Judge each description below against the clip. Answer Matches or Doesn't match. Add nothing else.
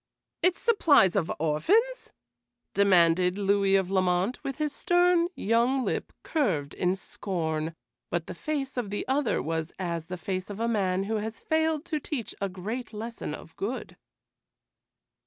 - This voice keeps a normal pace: Matches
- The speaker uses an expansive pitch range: Matches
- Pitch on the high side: Matches